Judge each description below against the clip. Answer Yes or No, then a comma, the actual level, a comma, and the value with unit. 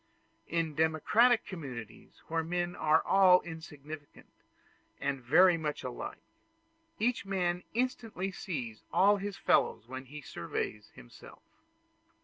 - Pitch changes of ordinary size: Yes, average, 5.0 semitones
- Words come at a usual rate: No, slow, 115 wpm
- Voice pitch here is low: No, medium, 165 Hz